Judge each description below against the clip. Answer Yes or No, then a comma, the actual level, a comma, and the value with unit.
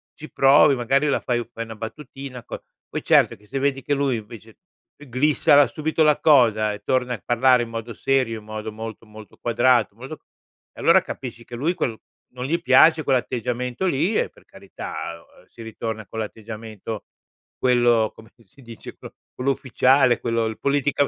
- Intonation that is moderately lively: Yes, average, 3.4 semitones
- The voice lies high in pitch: No, low, 120 Hz